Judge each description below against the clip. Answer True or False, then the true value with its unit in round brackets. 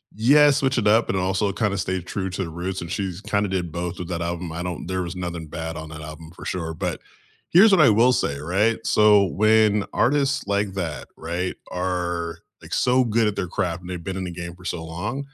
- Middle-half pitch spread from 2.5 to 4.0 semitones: True (3.7 semitones)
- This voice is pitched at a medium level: False (95 Hz)